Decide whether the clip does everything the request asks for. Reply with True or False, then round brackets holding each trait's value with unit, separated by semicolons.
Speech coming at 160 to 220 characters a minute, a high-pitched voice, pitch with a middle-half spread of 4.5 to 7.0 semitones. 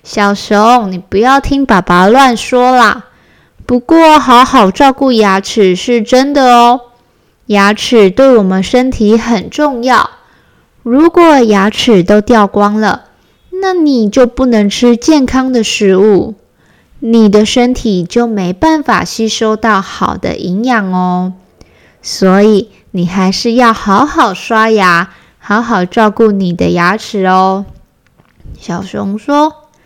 False (180 characters per minute; 225 Hz; 4.1 semitones)